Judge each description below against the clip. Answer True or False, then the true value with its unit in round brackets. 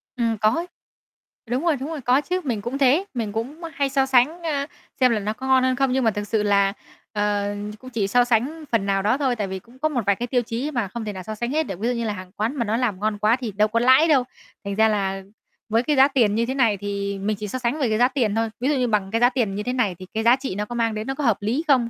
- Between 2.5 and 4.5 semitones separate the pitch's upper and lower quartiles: True (4.0 semitones)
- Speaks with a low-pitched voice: False (235 Hz)